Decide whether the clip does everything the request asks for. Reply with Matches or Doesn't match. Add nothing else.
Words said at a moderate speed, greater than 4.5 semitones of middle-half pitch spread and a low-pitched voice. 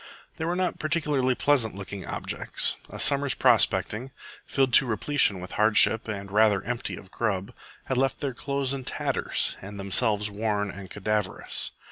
Matches